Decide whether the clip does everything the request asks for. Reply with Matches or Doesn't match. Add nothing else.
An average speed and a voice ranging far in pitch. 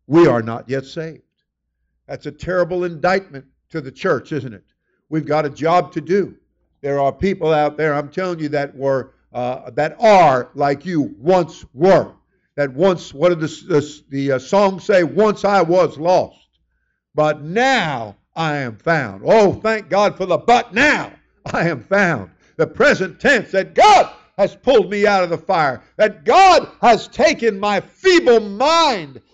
Matches